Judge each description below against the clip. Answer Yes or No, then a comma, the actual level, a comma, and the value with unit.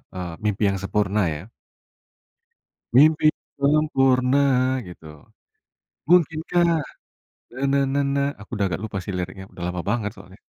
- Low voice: Yes, low, 125 Hz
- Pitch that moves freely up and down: Yes, wide, 6.8 semitones